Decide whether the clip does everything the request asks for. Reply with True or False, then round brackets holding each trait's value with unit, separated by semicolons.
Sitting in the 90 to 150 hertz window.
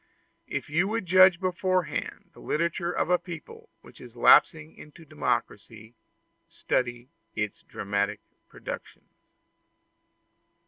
False (160 Hz)